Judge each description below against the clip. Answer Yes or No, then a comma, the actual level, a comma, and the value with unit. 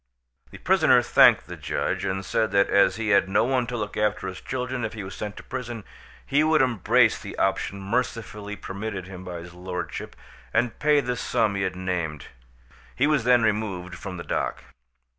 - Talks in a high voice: No, low, 105 Hz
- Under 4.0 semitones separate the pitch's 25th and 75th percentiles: No, average, 4.5 semitones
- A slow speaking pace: No, average, 195 wpm